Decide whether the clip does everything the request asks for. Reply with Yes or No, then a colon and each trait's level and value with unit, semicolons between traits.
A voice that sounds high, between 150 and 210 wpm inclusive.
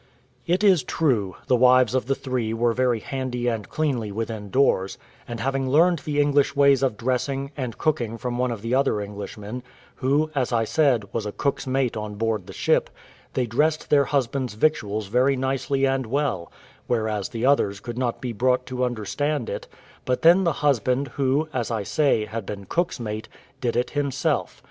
No: low, 125 Hz; average, 185 wpm